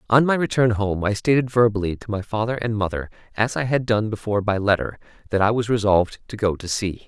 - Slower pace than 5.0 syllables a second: No, 6.1 syllables/s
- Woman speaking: No, male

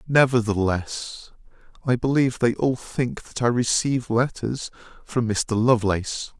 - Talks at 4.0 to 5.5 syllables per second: Yes, 4.5 syllables/s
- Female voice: No, male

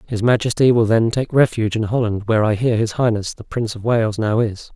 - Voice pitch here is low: Yes, low, 110 Hz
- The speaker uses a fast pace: Yes, fast, 240 wpm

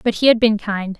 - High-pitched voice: Yes, high, 215 Hz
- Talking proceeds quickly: Yes, fast, 300 wpm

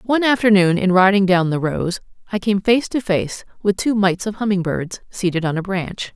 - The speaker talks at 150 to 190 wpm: No, fast, 205 wpm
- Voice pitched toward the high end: Yes, high, 195 Hz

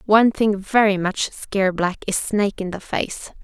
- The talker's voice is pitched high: Yes, high, 200 Hz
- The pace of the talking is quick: No, average, 190 wpm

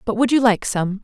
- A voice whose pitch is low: No, high, 220 Hz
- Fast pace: Yes, fast, 290 wpm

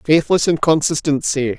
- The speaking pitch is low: No, medium, 150 Hz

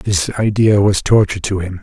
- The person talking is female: No, male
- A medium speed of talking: Yes, average, 195 wpm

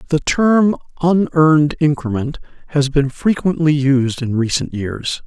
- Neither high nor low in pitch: Yes, medium, 150 Hz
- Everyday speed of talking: No, slow, 125 wpm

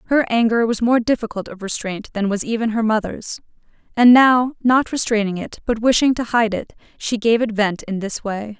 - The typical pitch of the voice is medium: No, high, 225 Hz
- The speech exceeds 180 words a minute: Yes, average, 195 wpm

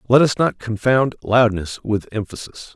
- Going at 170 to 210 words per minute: No, average, 155 wpm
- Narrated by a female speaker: No, male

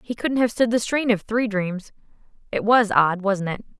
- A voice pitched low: No, high, 215 Hz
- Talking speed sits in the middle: No, fast, 220 wpm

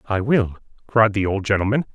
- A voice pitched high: No, low, 105 Hz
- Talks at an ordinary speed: Yes, average, 185 wpm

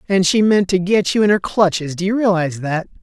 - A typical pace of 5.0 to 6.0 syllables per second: Yes, 5.8 syllables/s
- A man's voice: Yes, male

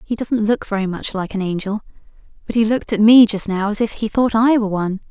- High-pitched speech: Yes, high, 210 Hz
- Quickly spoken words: Yes, fast, 260 wpm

